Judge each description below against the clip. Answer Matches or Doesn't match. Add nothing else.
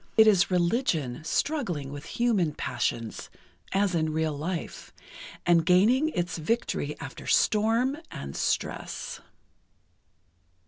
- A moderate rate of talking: Doesn't match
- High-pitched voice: Doesn't match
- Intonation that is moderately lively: Doesn't match